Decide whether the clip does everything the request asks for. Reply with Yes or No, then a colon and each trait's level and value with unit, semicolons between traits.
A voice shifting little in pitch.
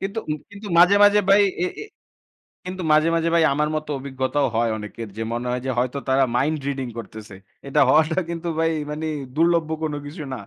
No: average, 4.2 semitones